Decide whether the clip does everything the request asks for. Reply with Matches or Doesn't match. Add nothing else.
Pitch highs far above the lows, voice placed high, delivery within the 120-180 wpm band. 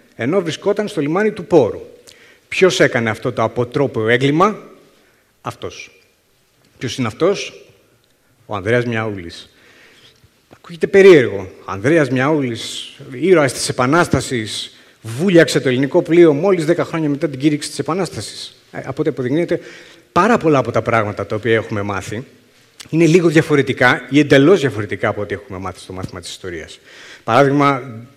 Doesn't match